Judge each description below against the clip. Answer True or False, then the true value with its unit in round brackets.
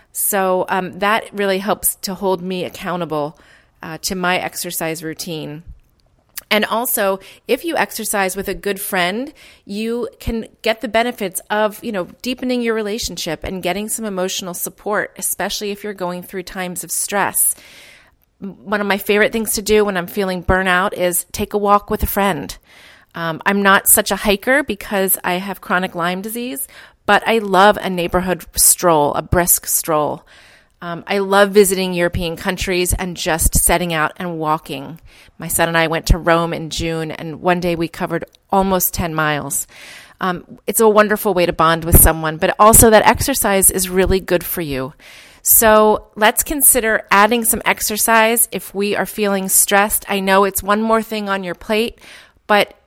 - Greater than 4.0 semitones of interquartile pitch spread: False (3.3 semitones)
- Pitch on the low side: False (190 Hz)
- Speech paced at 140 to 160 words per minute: False (175 wpm)